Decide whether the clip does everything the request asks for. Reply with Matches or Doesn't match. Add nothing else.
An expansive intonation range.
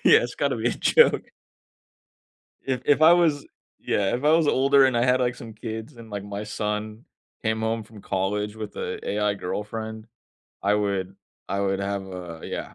Doesn't match